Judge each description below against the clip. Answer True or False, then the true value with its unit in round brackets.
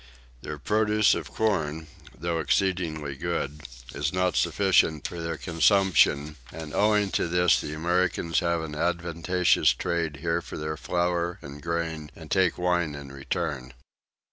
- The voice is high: False (85 Hz)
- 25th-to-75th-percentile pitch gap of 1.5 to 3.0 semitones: True (2.6 semitones)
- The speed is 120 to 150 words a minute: True (140 wpm)